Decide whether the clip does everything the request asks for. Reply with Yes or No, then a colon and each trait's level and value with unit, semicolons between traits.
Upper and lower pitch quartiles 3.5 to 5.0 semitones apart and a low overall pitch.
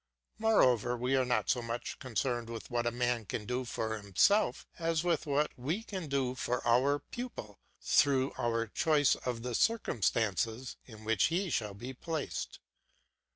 Yes: average, 4.1 semitones; low, 125 Hz